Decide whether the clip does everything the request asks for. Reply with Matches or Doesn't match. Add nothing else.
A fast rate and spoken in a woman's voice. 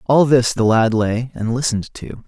Doesn't match